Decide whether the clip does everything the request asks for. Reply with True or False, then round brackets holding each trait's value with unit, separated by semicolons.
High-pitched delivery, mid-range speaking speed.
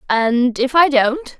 True (265 Hz; 170 wpm)